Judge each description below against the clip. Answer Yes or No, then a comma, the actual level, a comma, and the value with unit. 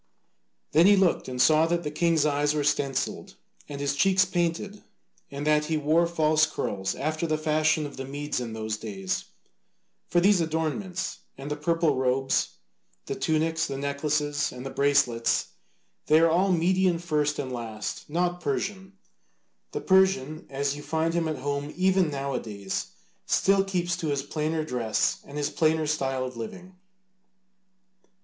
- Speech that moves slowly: No, average, 165 wpm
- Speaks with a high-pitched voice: No, medium, 155 Hz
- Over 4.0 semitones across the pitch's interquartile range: No, average, 3.5 semitones